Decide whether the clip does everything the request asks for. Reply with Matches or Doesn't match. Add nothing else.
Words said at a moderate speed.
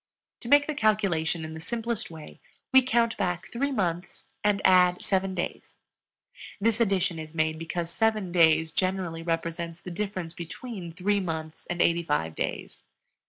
Matches